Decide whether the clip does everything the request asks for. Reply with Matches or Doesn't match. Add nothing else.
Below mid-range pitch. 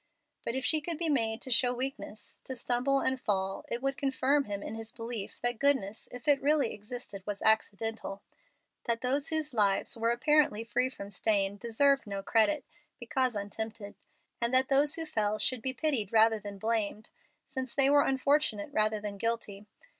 Doesn't match